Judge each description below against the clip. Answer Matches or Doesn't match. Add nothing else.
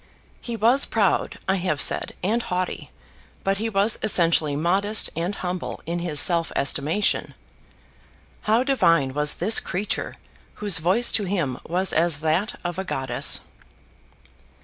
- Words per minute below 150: Matches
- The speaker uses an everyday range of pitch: Matches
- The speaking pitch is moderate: Matches